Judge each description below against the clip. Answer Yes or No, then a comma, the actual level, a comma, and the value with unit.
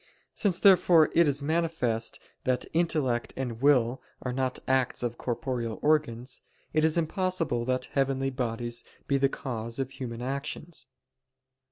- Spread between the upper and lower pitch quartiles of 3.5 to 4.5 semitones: Yes, average, 4.2 semitones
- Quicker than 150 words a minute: No, average, 140 wpm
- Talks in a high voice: No, low, 135 Hz